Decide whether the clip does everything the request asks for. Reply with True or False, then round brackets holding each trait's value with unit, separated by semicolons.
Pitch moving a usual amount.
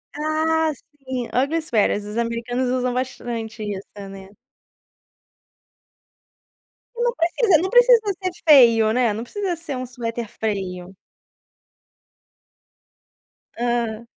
False (6.0 semitones)